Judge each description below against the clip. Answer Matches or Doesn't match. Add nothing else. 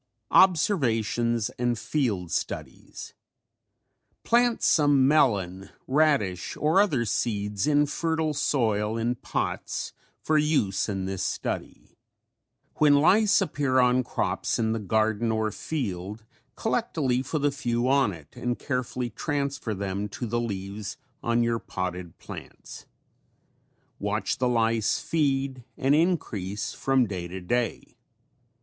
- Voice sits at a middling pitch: Doesn't match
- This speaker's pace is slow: Matches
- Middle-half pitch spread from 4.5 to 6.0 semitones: Matches